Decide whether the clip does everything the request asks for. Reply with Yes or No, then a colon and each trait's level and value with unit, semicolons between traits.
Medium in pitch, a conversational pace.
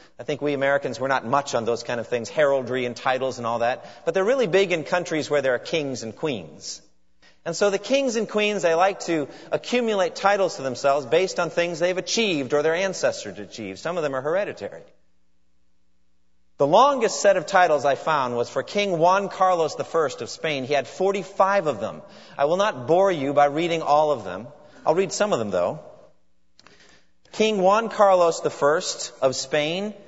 Yes: medium, 150 Hz; average, 195 wpm